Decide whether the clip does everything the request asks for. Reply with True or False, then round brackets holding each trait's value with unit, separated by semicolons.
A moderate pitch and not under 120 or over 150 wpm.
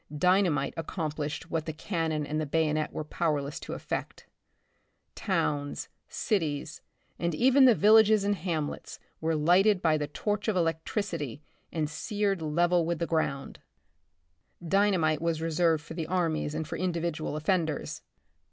True (165 Hz; 145 wpm)